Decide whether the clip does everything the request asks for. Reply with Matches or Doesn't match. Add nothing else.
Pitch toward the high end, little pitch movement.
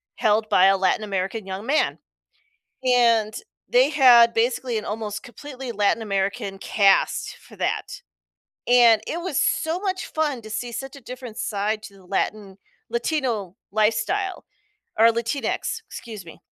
Doesn't match